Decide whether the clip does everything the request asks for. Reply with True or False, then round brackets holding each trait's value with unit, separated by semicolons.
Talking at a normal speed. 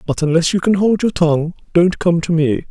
False (245 wpm)